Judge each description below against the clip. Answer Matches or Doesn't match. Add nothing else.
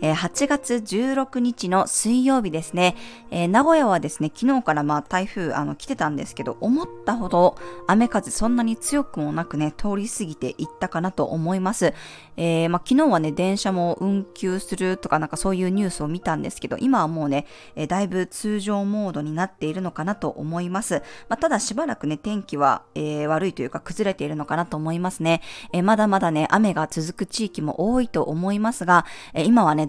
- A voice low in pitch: Doesn't match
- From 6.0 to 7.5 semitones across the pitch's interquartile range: Doesn't match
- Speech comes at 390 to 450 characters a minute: Matches